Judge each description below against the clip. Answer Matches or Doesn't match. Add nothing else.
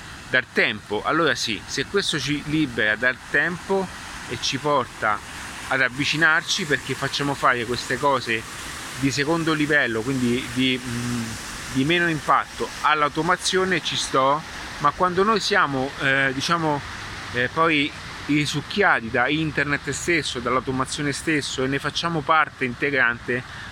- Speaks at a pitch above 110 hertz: Matches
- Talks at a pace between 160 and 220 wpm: Doesn't match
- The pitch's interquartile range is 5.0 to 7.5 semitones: Doesn't match